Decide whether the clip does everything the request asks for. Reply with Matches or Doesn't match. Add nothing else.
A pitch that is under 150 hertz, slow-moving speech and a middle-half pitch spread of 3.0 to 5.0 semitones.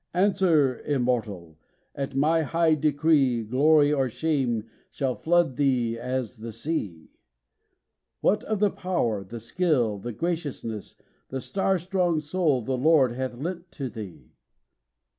Doesn't match